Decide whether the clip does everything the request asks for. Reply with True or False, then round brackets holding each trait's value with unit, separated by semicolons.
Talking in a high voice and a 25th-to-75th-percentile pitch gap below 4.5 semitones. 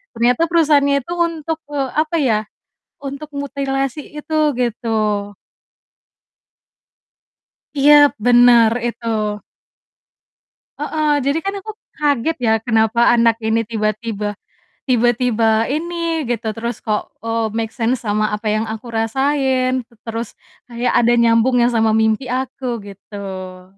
True (240 Hz; 3.9 semitones)